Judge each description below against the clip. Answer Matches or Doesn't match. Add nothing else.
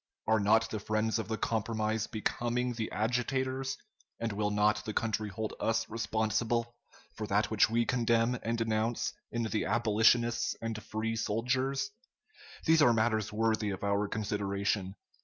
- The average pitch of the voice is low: Matches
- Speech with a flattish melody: Matches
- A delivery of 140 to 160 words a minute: Matches